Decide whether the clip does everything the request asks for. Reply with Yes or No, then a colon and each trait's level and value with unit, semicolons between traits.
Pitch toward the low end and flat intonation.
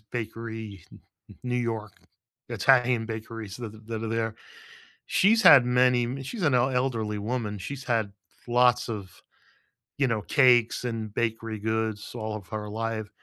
Yes: low, 115 Hz; narrow, 2.2 semitones